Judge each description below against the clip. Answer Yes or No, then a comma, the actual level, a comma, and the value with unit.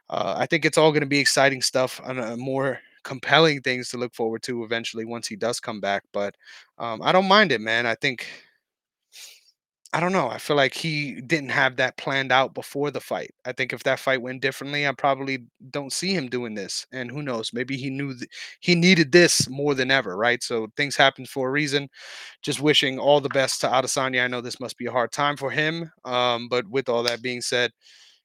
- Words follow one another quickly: Yes, fast, 225 wpm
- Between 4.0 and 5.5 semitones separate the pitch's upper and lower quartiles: No, average, 2.8 semitones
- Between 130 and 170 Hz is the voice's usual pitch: Yes, low, 135 Hz